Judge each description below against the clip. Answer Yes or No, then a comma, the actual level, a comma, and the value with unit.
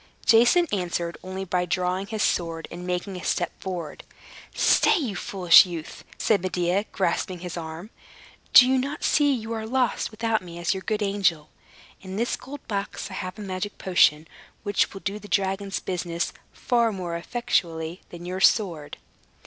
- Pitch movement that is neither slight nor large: Yes, average, 3.6 semitones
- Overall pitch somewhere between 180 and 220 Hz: Yes, high, 190 Hz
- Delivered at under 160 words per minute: No, average, 165 wpm